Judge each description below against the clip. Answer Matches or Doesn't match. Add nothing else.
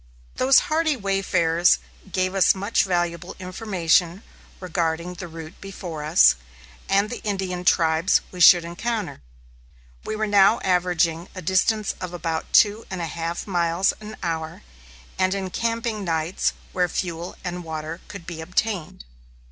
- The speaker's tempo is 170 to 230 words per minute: Doesn't match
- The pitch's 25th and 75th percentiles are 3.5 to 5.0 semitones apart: Doesn't match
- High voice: Doesn't match